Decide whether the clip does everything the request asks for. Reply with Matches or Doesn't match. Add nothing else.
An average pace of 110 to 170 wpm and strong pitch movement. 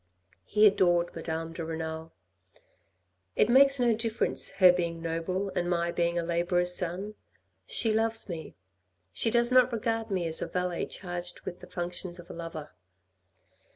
Doesn't match